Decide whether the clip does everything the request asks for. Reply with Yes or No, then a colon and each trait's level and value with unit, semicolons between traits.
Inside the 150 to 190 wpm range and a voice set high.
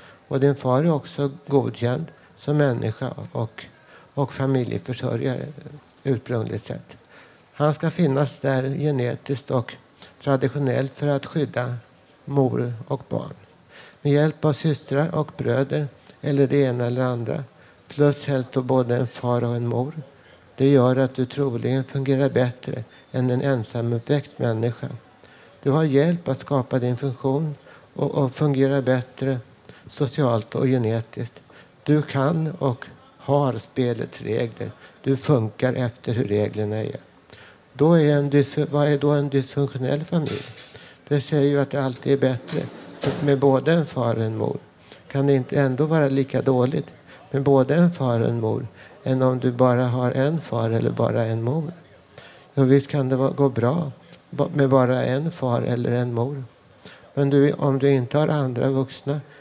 No: average, 155 wpm; low, 135 Hz